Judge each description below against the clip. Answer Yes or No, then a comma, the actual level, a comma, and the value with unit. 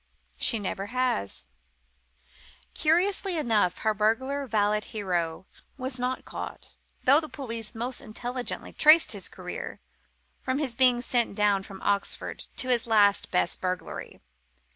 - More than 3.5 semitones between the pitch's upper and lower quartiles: Yes, average, 4.2 semitones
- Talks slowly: Yes, slow, 130 wpm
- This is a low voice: No, high, 230 Hz